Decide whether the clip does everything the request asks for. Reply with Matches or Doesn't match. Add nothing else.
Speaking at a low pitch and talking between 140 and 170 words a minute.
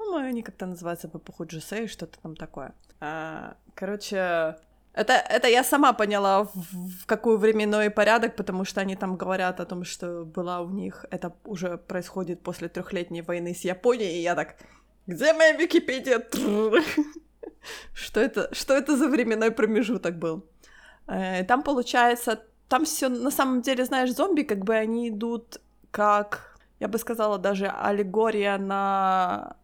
Doesn't match